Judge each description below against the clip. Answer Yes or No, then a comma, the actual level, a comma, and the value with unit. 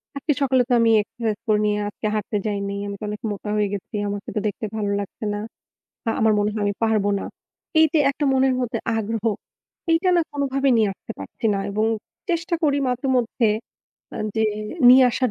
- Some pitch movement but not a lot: Yes, average, 4.0 semitones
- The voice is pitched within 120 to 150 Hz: No, high, 225 Hz